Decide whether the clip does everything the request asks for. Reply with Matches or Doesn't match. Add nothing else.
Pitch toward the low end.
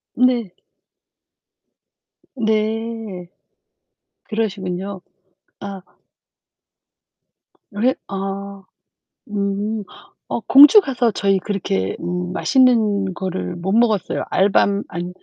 Doesn't match